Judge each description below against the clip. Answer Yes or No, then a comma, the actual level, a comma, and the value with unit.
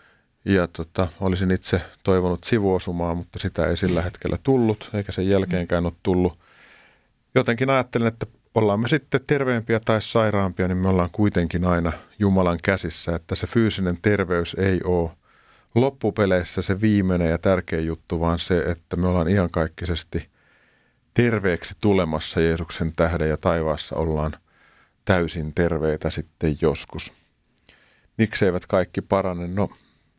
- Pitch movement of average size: Yes, average, 3.5 semitones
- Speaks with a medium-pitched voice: No, very low, 90 Hz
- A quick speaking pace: No, average, 135 wpm